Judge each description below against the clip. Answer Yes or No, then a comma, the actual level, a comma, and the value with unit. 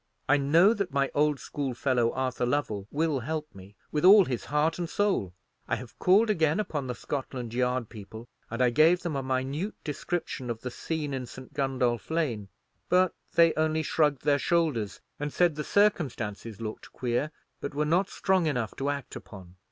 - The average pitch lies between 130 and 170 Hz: Yes, medium, 140 Hz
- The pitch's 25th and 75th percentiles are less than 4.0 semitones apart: No, average, 4.8 semitones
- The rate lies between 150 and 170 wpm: No, average, 185 wpm